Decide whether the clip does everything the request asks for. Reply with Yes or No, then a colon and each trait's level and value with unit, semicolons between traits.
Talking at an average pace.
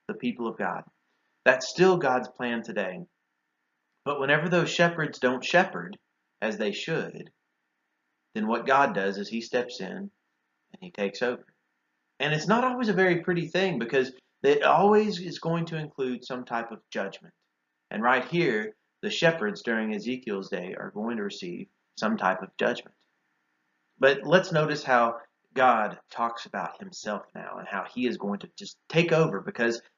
Yes: average, 170 wpm